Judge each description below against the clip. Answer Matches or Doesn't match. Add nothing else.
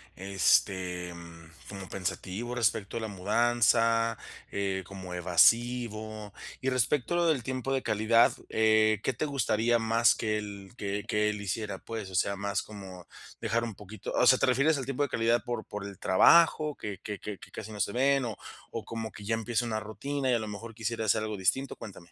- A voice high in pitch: Doesn't match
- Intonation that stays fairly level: Doesn't match